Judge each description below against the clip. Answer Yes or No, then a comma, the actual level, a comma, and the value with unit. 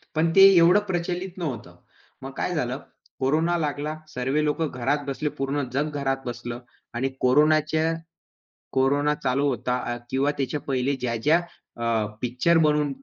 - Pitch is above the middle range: No, medium, 145 Hz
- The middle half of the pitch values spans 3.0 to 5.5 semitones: Yes, average, 3.5 semitones